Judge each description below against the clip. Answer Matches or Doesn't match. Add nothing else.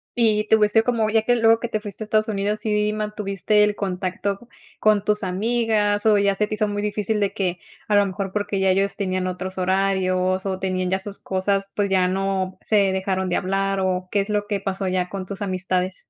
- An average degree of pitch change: Doesn't match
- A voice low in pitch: Doesn't match